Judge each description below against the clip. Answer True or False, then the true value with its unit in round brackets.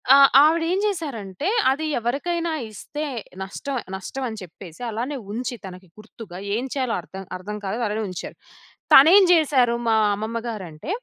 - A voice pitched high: True (235 Hz)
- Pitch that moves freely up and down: True (6.5 semitones)